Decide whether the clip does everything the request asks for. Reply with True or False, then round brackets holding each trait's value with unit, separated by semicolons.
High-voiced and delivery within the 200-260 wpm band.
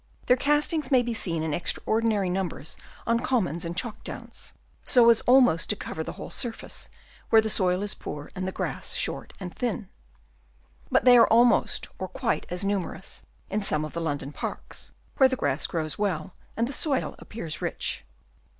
False (205 Hz; 180 wpm)